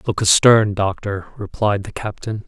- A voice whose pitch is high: No, low, 100 Hz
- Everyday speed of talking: Yes, average, 145 wpm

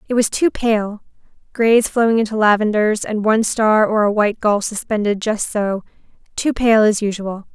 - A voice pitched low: No, high, 215 Hz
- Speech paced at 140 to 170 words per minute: Yes, average, 160 wpm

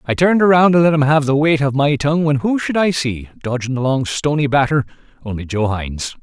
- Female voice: No, male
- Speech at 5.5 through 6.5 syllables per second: Yes, 6.0 syllables/s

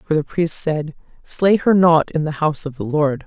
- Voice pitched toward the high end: No, medium, 155 Hz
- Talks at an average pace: No, fast, 240 wpm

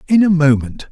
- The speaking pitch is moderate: Yes, medium, 160 Hz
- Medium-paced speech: Yes, average, 195 wpm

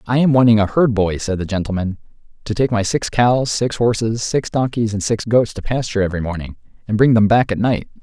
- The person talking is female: No, male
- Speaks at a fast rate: Yes, fast, 230 wpm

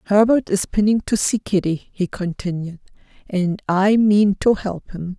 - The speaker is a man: No, female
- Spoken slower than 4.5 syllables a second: Yes, 4.3 syllables/s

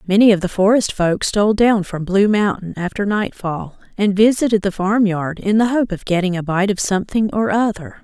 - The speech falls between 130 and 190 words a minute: No, average, 200 wpm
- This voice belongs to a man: No, female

